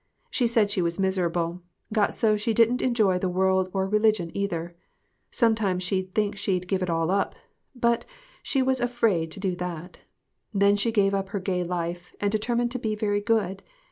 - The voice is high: Yes, high, 195 Hz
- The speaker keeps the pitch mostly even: No, average, 3.3 semitones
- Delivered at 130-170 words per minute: No, average, 185 wpm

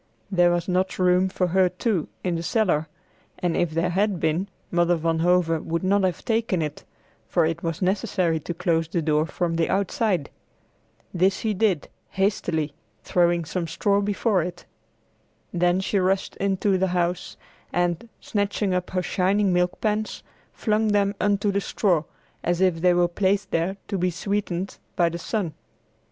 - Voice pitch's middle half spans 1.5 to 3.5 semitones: Yes, narrow, 2.6 semitones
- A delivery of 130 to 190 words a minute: Yes, average, 170 wpm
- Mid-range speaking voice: Yes, medium, 180 Hz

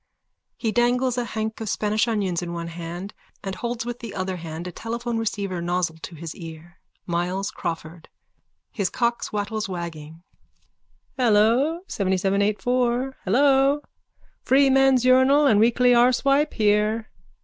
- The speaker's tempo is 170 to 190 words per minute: No, slow, 135 wpm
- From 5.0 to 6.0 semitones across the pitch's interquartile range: Yes, wide, 5.4 semitones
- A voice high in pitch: Yes, high, 215 Hz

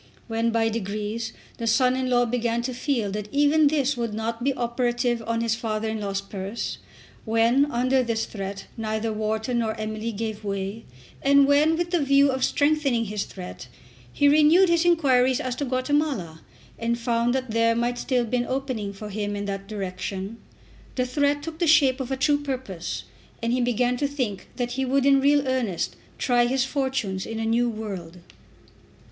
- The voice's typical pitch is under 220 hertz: No, high, 240 Hz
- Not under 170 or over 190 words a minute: Yes, average, 185 wpm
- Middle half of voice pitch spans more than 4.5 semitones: No, average, 3.6 semitones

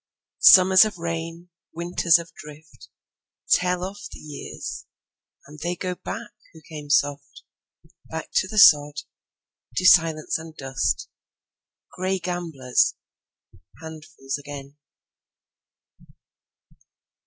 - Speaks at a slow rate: Yes, slow, 75 wpm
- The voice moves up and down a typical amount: Yes, average, 3.4 semitones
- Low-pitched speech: No, medium, 160 Hz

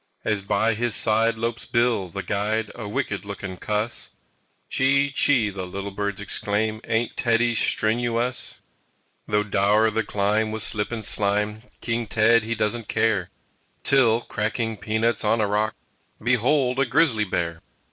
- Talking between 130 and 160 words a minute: Yes, average, 155 wpm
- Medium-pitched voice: No, low, 110 Hz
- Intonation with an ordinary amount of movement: No, narrow, 2.2 semitones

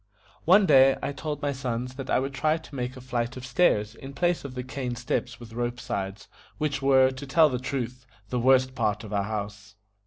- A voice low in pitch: Yes, low, 130 Hz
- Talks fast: Yes, fast, 220 wpm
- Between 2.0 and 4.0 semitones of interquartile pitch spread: Yes, narrow, 2.5 semitones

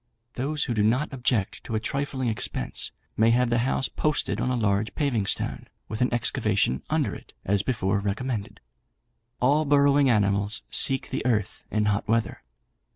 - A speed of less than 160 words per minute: No, average, 165 wpm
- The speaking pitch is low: Yes, low, 120 Hz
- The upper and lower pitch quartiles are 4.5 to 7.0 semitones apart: No, average, 4.1 semitones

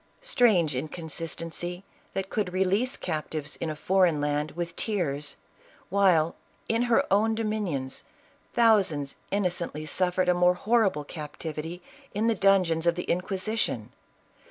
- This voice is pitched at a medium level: Yes, medium, 180 Hz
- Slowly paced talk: Yes, slow, 125 wpm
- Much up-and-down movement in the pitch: No, average, 4.2 semitones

